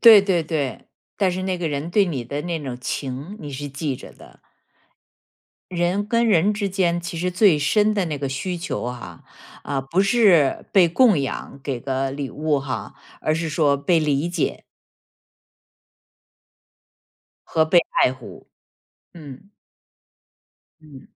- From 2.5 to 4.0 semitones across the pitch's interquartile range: No, average, 4.8 semitones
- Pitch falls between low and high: Yes, medium, 160 Hz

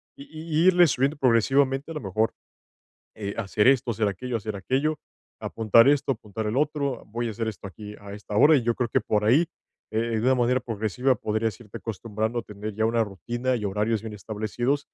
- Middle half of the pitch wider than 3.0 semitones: Yes, average, 3.7 semitones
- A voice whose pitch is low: Yes, low, 115 Hz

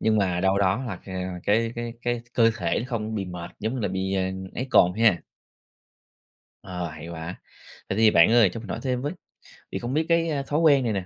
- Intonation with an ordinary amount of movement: Yes, average, 4.4 semitones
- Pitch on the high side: No, low, 110 Hz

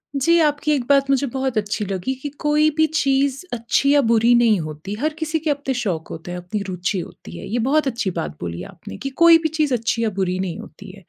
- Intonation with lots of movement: Yes, wide, 7.1 semitones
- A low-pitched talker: No, high, 245 Hz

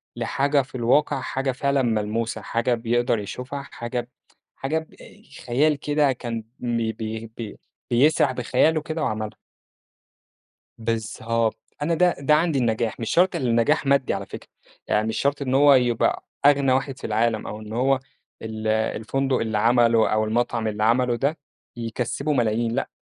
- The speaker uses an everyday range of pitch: Yes, average, 3.6 semitones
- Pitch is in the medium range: No, low, 120 Hz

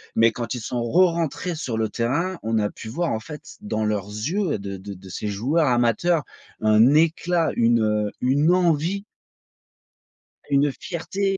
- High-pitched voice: No, low, 125 Hz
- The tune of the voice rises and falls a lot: Yes, wide, 7.4 semitones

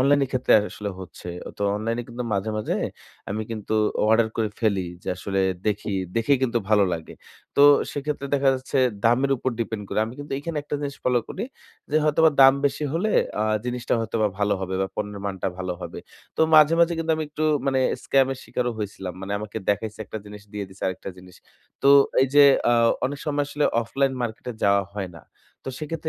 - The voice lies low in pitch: Yes, low, 115 Hz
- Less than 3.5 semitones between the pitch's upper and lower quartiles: No, wide, 5.5 semitones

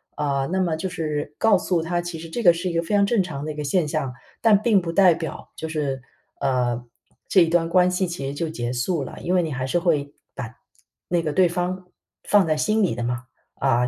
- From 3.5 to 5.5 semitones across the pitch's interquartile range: Yes, average, 4.2 semitones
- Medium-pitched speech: Yes, medium, 165 Hz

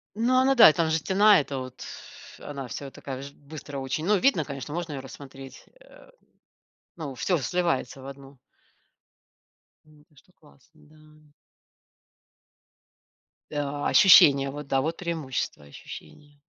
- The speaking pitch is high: No, medium, 145 Hz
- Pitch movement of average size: Yes, average, 3.4 semitones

